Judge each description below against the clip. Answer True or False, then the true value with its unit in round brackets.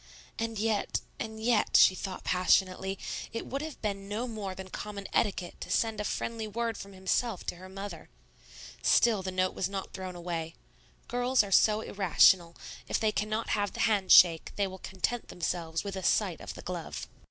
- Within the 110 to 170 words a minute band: False (185 wpm)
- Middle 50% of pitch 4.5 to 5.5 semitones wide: False (2.9 semitones)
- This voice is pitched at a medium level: False (200 Hz)